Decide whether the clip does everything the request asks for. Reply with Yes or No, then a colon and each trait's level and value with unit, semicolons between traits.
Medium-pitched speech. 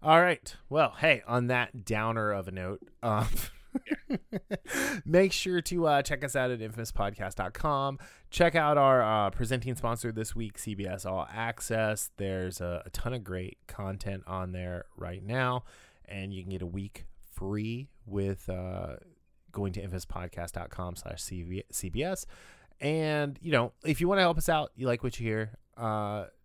No: low, 110 Hz